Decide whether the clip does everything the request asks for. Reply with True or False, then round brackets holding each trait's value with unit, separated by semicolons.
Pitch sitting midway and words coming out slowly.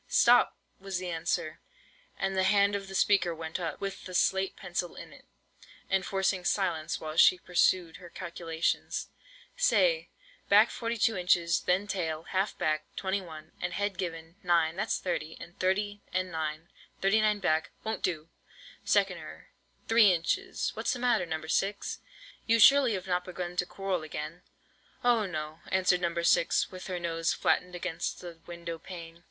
False (180 Hz; 155 wpm)